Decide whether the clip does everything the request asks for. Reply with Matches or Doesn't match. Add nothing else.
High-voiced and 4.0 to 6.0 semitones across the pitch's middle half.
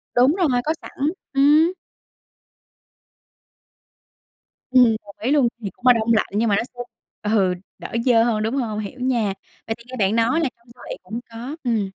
Doesn't match